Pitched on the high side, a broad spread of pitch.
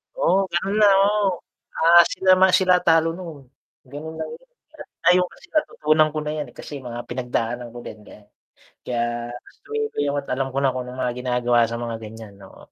No: medium, 140 Hz; wide, 6.8 semitones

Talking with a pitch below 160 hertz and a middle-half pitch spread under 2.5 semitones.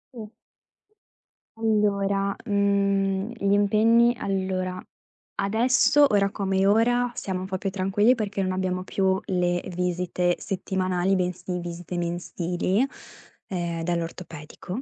No: high, 190 Hz; narrow, 2.0 semitones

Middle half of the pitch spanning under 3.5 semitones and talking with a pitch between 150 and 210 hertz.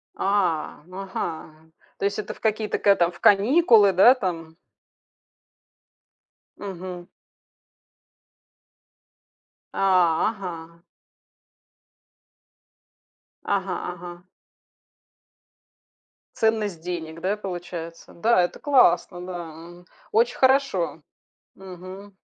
Yes: average, 3.0 semitones; medium, 185 Hz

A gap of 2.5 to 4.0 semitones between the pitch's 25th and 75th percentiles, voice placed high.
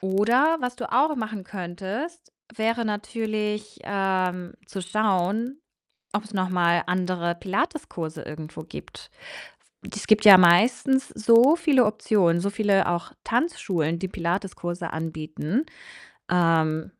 No: average, 4.7 semitones; high, 195 Hz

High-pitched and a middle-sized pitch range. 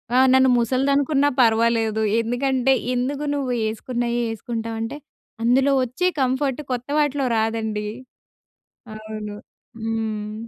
Yes: high, 240 Hz; average, 3.1 semitones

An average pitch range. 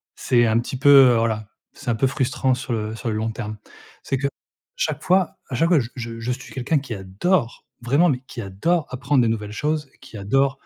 Yes: average, 3.6 semitones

